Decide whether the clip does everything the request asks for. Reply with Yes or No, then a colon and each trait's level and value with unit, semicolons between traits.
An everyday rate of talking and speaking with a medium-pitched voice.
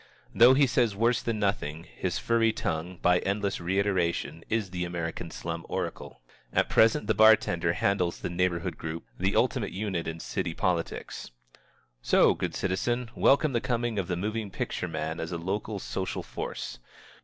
No: average, 170 wpm; very low, 95 Hz